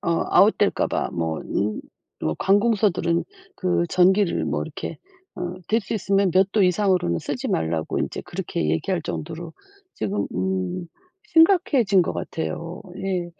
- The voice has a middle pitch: Yes, medium, 180 Hz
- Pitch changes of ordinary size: Yes, average, 4.5 semitones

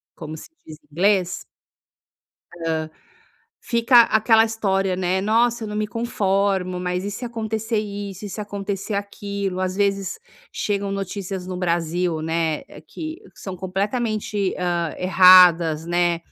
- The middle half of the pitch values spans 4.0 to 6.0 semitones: No, average, 2.7 semitones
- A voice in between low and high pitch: No, high, 195 Hz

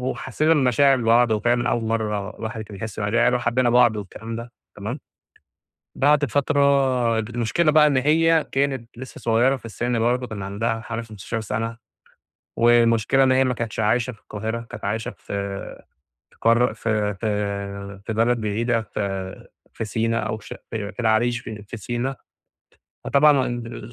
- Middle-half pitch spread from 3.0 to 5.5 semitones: No, narrow, 2.4 semitones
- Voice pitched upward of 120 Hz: No, low, 115 Hz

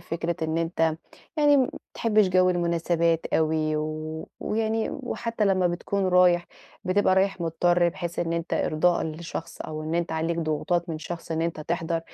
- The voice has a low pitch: No, medium, 170 Hz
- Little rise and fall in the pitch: Yes, narrow, 2.2 semitones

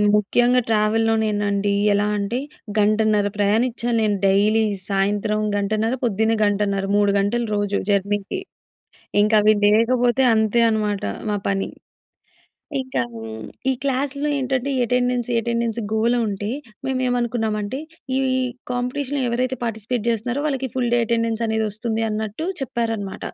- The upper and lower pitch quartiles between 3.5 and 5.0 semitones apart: No, average, 2.9 semitones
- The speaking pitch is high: Yes, high, 220 Hz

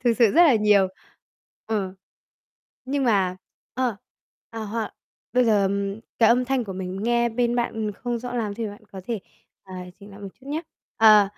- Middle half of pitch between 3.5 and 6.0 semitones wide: No, average, 3.1 semitones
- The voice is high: Yes, high, 225 Hz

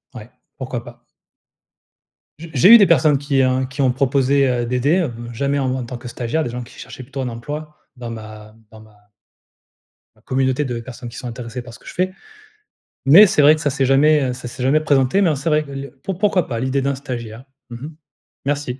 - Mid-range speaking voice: No, low, 130 Hz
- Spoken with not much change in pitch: No, average, 3.2 semitones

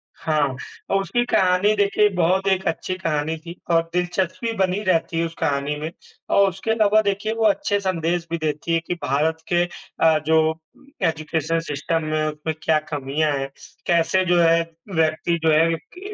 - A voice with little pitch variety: No, average, 3.2 semitones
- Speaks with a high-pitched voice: No, medium, 165 Hz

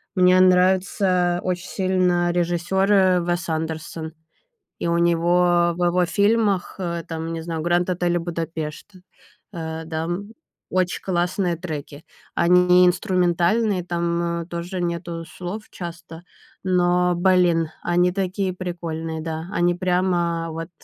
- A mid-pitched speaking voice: Yes, medium, 175 Hz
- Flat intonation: Yes, narrow, 1.4 semitones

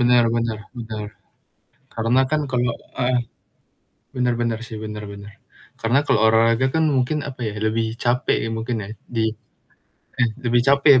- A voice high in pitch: No, low, 120 Hz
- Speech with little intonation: Yes, narrow, 2.1 semitones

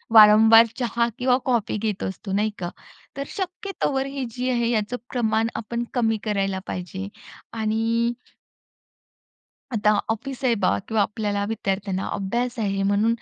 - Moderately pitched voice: No, high, 225 Hz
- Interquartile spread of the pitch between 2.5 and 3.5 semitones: Yes, average, 2.9 semitones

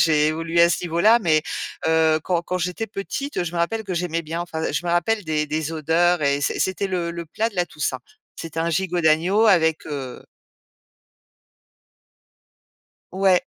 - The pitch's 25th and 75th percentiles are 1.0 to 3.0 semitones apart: Yes, narrow, 2.4 semitones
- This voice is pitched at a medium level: Yes, medium, 170 Hz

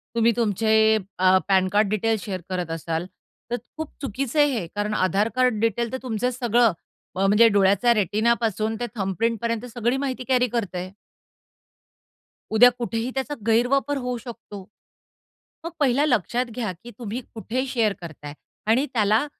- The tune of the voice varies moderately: Yes, average, 3.4 semitones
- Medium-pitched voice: No, high, 225 Hz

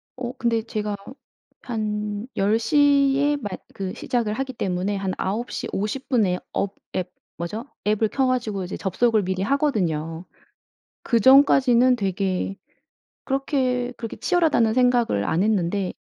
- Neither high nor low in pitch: No, high, 220 Hz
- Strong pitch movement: No, average, 4.7 semitones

